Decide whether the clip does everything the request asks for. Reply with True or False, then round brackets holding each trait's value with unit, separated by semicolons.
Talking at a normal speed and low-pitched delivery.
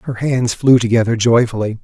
True (165 wpm; 115 Hz)